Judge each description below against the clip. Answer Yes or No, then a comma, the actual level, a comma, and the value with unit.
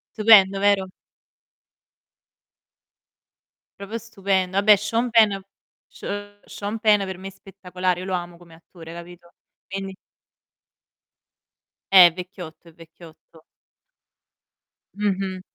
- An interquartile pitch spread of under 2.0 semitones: No, narrow, 2.5 semitones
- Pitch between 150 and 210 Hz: Yes, high, 190 Hz